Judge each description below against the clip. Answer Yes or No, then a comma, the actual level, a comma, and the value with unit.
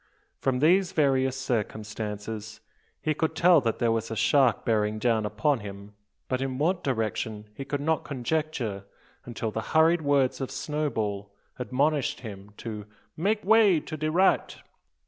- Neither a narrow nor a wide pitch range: No, wide, 6.0 semitones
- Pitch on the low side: Yes, low, 130 Hz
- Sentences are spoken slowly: No, average, 150 wpm